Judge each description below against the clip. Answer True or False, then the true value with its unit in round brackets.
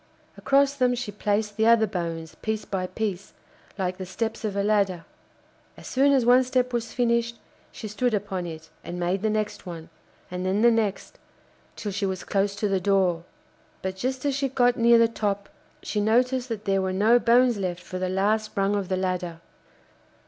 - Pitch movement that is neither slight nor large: True (3.9 semitones)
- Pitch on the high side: True (205 Hz)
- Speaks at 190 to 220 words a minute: True (195 wpm)